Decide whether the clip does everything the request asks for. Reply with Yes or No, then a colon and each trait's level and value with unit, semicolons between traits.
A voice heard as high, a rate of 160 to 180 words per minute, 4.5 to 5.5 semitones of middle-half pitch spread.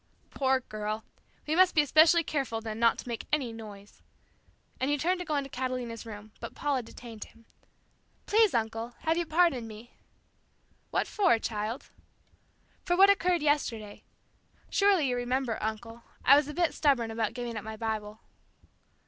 Yes: high, 245 Hz; average, 165 wpm; average, 5.2 semitones